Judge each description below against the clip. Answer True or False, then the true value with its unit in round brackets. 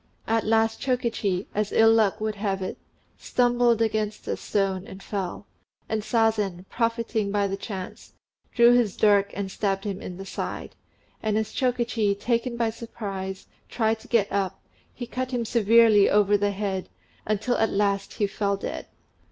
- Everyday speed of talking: True (165 wpm)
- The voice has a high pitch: True (215 Hz)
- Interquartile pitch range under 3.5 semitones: True (2.5 semitones)